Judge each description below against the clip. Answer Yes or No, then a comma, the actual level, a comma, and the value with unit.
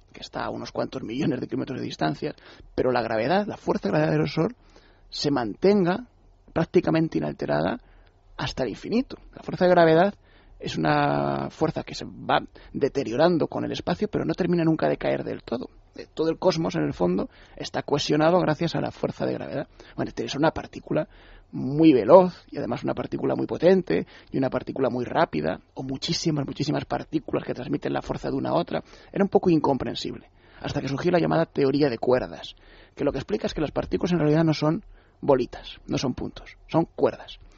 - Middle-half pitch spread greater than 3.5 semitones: Yes, average, 4.4 semitones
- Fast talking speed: Yes, fast, 195 wpm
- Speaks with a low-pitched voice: No, medium, 160 Hz